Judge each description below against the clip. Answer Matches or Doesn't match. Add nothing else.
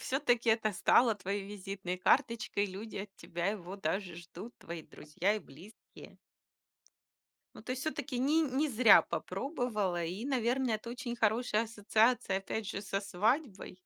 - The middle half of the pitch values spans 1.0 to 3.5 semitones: Doesn't match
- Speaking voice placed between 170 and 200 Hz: Doesn't match